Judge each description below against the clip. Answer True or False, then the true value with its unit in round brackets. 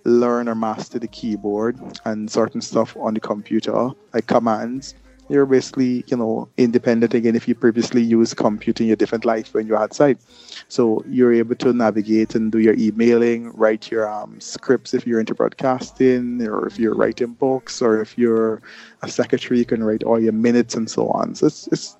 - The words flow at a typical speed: True (190 wpm)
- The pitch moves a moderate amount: False (1.7 semitones)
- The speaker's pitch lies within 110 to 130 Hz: True (115 Hz)